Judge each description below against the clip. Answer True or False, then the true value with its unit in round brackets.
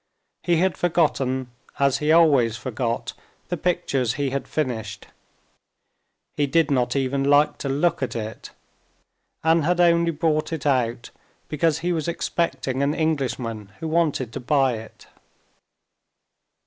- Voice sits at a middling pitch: True (145 Hz)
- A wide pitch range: False (4.2 semitones)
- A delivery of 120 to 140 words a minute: True (135 wpm)